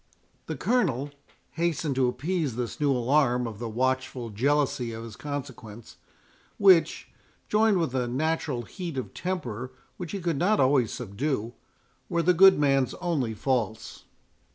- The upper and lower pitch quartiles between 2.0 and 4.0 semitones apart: No, average, 5.3 semitones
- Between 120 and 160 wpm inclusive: Yes, average, 145 wpm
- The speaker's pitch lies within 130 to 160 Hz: Yes, low, 135 Hz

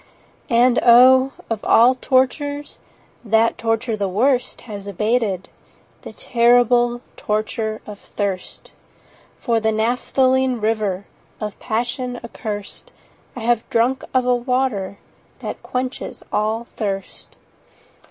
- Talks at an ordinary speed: No, slow, 115 wpm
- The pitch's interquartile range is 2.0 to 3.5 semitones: Yes, average, 2.8 semitones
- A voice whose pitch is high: Yes, high, 235 Hz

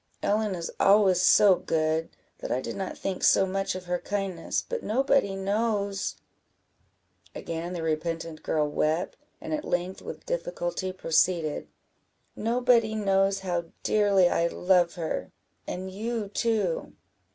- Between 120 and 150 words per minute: Yes, average, 140 wpm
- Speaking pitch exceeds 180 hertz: Yes, high, 190 Hz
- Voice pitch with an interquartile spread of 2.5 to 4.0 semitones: Yes, average, 3.6 semitones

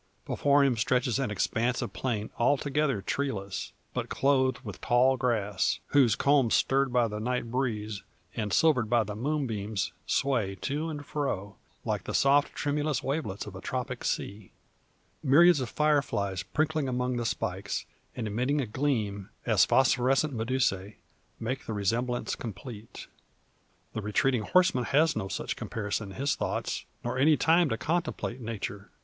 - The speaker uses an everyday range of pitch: Yes, average, 4.8 semitones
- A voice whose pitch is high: No, low, 125 Hz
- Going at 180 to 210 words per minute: No, average, 155 wpm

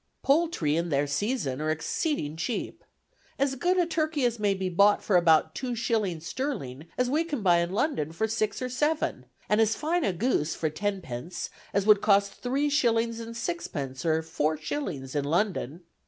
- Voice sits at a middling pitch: No, high, 200 Hz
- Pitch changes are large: Yes, wide, 8.1 semitones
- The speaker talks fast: No, average, 180 wpm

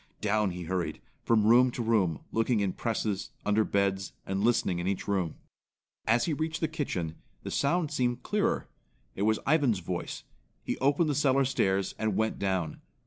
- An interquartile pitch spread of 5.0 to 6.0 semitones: Yes, wide, 5.4 semitones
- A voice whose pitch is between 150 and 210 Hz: No, low, 110 Hz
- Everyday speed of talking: Yes, average, 175 wpm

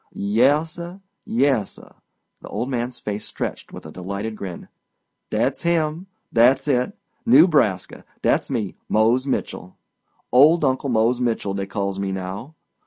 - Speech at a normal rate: No, slow, 115 wpm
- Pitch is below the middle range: Yes, low, 120 Hz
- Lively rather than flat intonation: Yes, wide, 6.7 semitones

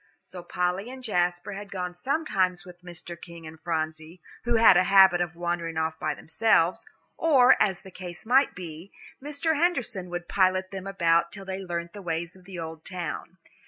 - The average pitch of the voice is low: No, medium, 180 Hz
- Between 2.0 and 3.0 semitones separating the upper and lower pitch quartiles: Yes, narrow, 2.4 semitones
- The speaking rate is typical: Yes, average, 185 wpm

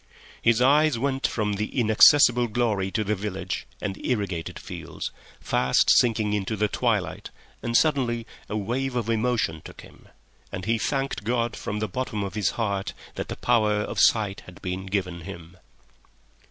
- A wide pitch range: No, average, 3.7 semitones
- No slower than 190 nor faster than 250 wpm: No, average, 165 wpm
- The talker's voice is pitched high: No, low, 110 Hz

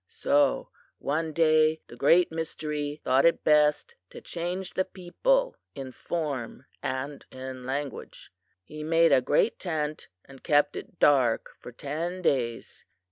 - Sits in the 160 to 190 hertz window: No, medium, 150 Hz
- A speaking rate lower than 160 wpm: Yes, slow, 135 wpm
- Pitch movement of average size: Yes, average, 3.7 semitones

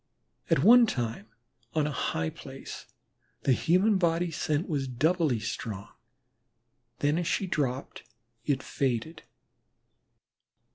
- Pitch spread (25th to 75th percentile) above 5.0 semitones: Yes, wide, 5.5 semitones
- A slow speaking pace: Yes, slow, 110 wpm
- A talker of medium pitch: Yes, medium, 150 Hz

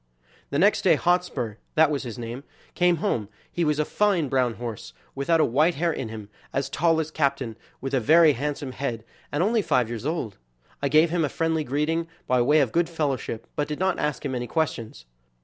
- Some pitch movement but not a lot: Yes, average, 4.7 semitones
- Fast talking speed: Yes, fast, 210 wpm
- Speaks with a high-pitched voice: No, medium, 145 Hz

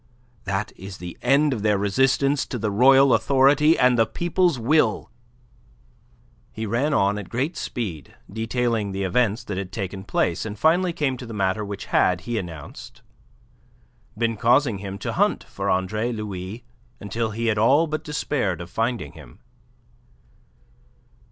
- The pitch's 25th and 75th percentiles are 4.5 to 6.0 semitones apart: Yes, average, 5.1 semitones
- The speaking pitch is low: Yes, low, 110 Hz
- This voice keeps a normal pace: Yes, average, 155 wpm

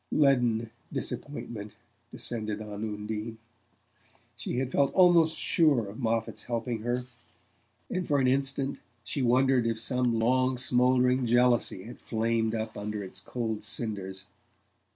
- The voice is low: Yes, low, 120 Hz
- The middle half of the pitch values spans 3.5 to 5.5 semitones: No, average, 2.8 semitones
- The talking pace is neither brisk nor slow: No, slow, 130 wpm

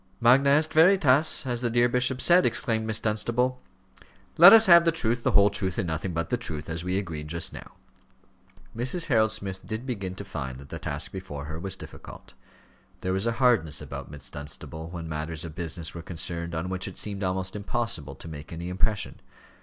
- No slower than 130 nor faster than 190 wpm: No, average, 200 wpm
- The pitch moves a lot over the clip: Yes, wide, 6.6 semitones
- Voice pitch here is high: No, very low, 95 Hz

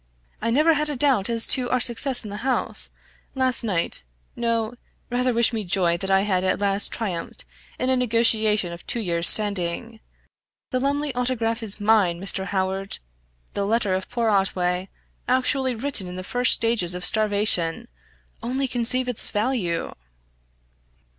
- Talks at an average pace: Yes, average, 160 wpm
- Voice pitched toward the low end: No, high, 220 Hz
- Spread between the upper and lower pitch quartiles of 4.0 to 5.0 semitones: Yes, average, 4.5 semitones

